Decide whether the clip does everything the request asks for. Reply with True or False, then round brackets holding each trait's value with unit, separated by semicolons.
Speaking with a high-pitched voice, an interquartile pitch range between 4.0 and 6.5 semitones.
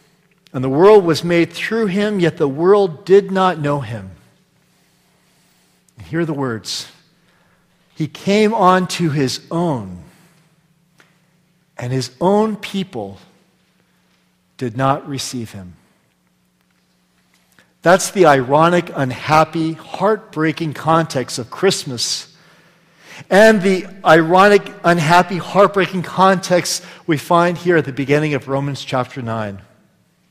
False (165 Hz; 5.5 semitones)